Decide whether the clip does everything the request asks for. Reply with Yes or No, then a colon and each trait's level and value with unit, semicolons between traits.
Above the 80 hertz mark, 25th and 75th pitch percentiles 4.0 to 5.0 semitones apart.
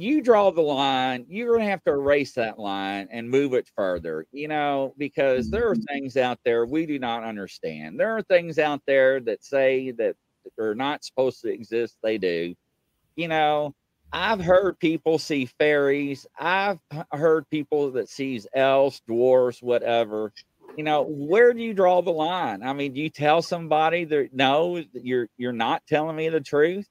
Yes: medium, 140 Hz; average, 4.5 semitones